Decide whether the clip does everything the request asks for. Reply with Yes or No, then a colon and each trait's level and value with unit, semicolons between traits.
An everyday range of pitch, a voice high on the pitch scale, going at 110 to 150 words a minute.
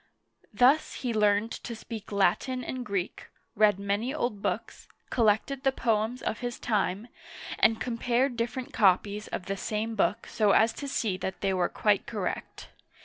No: average, 3.3 semitones; high, 220 Hz; average, 160 wpm